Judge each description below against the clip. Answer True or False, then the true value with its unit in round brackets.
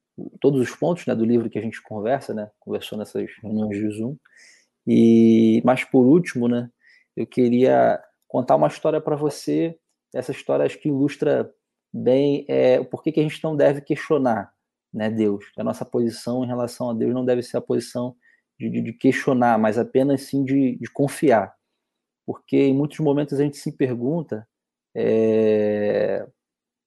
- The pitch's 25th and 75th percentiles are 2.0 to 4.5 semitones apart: True (4.0 semitones)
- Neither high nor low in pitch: False (125 Hz)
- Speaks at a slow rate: False (170 wpm)